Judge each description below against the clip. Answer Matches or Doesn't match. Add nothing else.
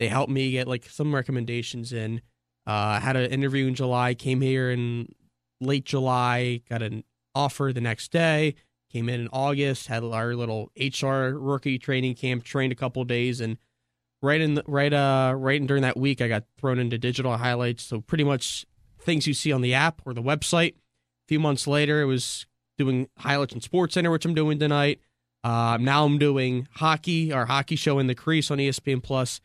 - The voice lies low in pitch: Matches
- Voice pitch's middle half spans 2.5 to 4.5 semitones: Matches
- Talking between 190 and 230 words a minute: Matches